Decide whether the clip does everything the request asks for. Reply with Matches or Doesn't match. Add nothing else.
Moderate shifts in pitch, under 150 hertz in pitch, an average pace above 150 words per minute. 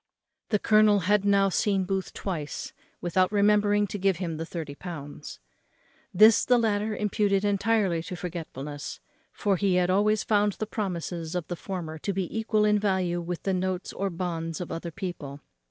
Doesn't match